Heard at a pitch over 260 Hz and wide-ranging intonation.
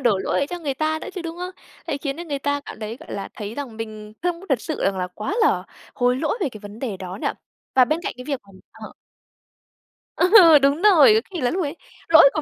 Yes: very high, 280 Hz; wide, 6.6 semitones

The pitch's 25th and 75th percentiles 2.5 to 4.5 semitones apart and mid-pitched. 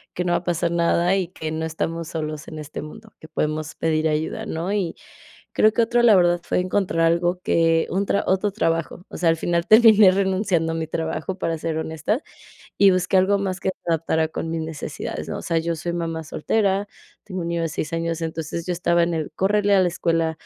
Yes: average, 2.8 semitones; medium, 170 Hz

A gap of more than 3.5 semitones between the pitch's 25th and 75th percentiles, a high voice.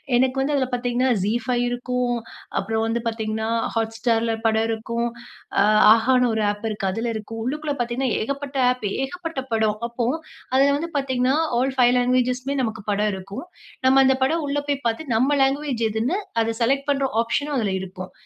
No: average, 3.2 semitones; high, 245 Hz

